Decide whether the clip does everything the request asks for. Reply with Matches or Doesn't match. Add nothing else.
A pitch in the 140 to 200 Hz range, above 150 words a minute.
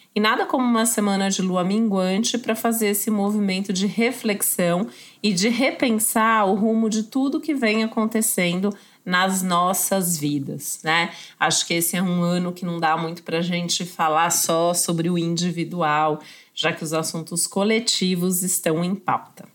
Matches